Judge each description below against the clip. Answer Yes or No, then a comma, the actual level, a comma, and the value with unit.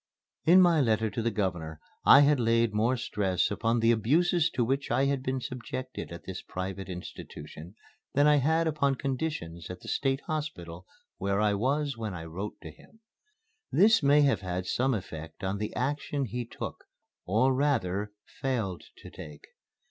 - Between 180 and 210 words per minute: No, average, 170 wpm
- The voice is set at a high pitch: No, low, 115 Hz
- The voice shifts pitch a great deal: Yes, wide, 6.7 semitones